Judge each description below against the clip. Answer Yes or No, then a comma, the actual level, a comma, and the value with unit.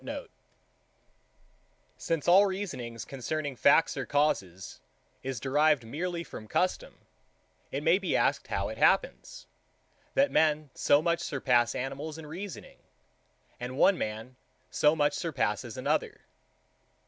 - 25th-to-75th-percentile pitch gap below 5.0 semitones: Yes, average, 4.6 semitones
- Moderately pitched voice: Yes, medium, 150 Hz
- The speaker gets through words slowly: Yes, slow, 120 wpm